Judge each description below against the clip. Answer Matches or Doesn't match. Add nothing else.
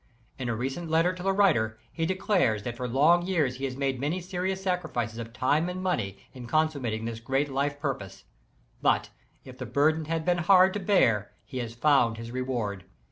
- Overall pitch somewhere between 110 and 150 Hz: Matches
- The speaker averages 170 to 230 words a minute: Matches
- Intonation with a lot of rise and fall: Matches